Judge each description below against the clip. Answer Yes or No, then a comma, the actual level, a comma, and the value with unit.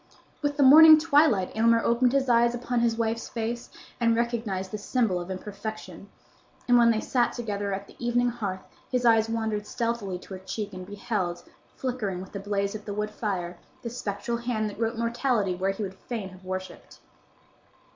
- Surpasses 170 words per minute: Yes, average, 185 wpm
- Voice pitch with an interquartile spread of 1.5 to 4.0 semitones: Yes, average, 3.3 semitones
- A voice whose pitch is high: Yes, high, 220 Hz